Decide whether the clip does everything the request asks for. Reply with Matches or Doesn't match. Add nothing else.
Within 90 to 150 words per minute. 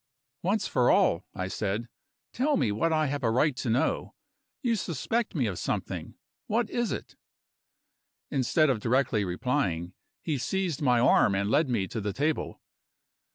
Doesn't match